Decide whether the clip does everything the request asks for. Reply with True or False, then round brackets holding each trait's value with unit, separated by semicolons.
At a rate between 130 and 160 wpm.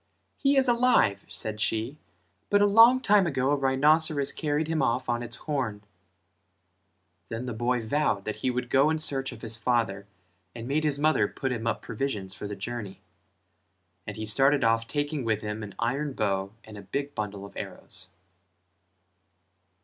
False (175 wpm)